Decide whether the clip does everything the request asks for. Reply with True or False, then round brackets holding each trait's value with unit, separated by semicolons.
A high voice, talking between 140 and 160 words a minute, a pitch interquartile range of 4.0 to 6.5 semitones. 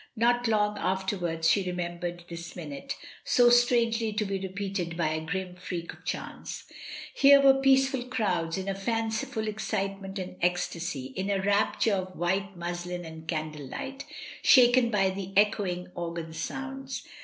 True (195 Hz; 150 wpm; 4.4 semitones)